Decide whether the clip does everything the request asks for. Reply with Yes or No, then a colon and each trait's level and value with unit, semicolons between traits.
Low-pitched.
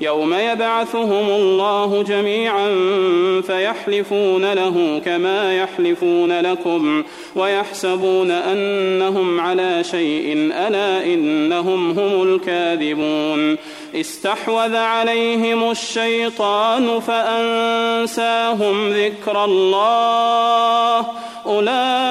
No: high, 205 Hz